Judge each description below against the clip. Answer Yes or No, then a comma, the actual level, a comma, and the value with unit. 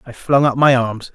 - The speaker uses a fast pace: Yes, fast, 260 wpm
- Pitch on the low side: Yes, low, 130 Hz